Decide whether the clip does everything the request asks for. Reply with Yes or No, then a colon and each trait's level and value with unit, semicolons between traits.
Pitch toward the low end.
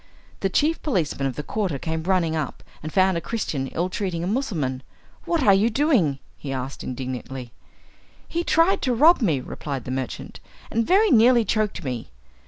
No: medium, 180 Hz